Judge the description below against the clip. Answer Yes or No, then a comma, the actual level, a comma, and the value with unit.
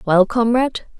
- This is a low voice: No, high, 225 Hz